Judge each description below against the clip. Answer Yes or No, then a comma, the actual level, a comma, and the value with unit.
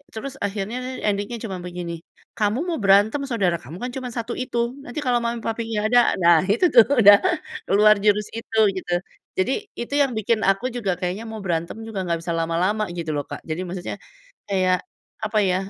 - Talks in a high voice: Yes, high, 205 Hz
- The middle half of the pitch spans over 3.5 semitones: Yes, average, 4.3 semitones